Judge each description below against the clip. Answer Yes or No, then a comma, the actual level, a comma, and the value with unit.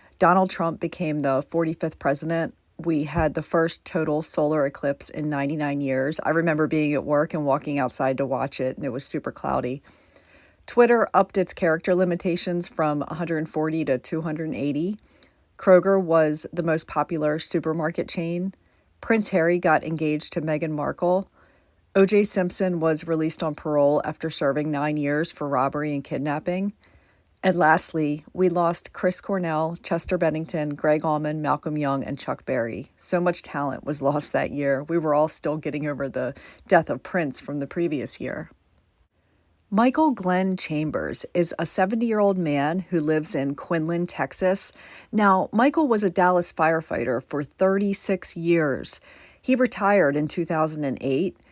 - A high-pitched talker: No, medium, 160 Hz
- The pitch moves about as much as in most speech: Yes, average, 3.3 semitones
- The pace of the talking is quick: No, average, 155 wpm